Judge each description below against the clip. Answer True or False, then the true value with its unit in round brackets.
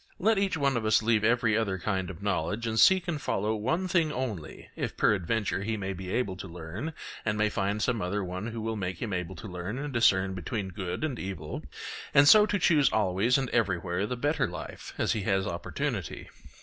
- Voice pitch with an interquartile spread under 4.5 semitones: False (5.0 semitones)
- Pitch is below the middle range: True (105 Hz)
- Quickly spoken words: True (210 wpm)